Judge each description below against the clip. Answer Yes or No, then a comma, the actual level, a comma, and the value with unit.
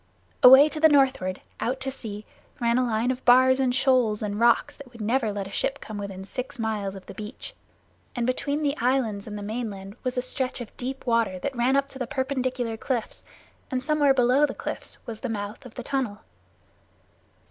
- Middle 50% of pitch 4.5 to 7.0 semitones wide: No, average, 3.6 semitones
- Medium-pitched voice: No, very high, 250 Hz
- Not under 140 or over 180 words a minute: No, fast, 205 wpm